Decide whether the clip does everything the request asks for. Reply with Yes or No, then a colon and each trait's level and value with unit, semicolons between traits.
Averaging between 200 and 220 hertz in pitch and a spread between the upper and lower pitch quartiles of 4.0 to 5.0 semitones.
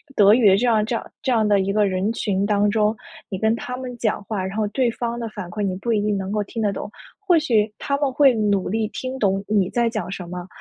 No: high, 215 Hz; average, 2.8 semitones